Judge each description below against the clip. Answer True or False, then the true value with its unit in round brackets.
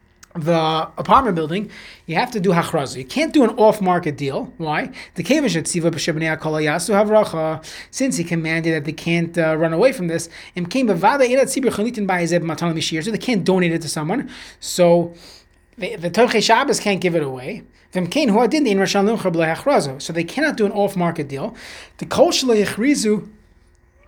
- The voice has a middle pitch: True (175 Hz)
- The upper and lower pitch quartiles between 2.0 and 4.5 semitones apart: False (4.9 semitones)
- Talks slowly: True (120 wpm)